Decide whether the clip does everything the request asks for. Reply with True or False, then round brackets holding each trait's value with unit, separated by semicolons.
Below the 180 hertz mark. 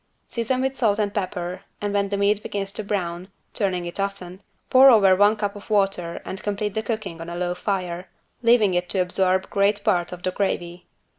False (200 Hz)